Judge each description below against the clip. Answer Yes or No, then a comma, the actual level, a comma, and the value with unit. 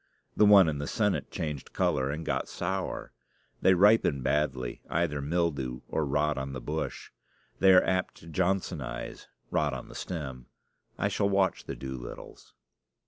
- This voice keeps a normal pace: Yes, average, 155 wpm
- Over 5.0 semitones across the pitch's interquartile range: Yes, wide, 5.5 semitones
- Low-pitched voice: Yes, very low, 75 Hz